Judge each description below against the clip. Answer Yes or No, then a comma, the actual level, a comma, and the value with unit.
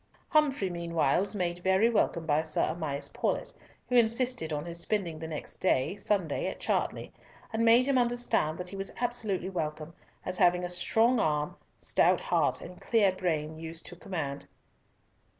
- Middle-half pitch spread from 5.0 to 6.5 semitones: Yes, wide, 5.6 semitones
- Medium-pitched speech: Yes, medium, 180 Hz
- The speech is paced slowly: No, average, 170 wpm